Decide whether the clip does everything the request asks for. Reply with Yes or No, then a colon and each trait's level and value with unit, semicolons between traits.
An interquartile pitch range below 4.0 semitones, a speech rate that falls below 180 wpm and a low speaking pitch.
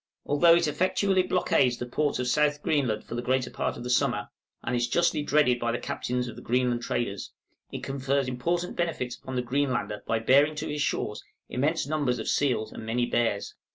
No: average, 3.6 semitones; average, 200 wpm; low, 130 Hz